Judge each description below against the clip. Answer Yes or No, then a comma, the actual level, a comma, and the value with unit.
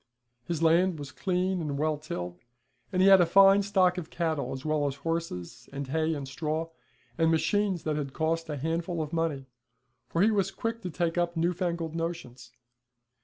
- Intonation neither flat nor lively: Yes, average, 3.1 semitones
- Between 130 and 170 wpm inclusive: No, average, 190 wpm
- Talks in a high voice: No, medium, 165 Hz